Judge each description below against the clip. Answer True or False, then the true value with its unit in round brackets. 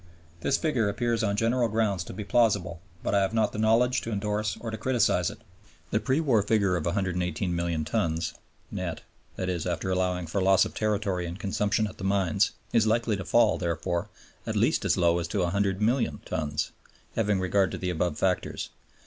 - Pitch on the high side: False (100 Hz)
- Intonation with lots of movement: False (3.7 semitones)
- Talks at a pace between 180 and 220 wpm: True (190 wpm)